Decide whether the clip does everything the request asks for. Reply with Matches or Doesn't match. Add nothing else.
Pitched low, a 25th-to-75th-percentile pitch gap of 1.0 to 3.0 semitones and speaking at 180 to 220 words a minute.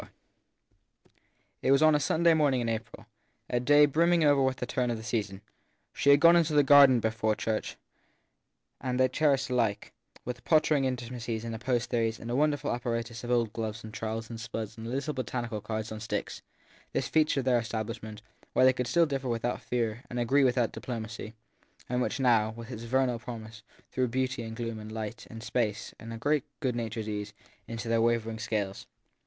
Matches